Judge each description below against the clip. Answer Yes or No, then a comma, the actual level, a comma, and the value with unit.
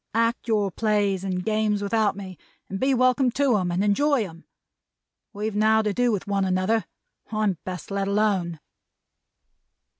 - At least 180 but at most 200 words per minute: No, average, 155 wpm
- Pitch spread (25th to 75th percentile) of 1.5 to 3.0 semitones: Yes, narrow, 2.4 semitones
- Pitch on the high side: Yes, high, 205 Hz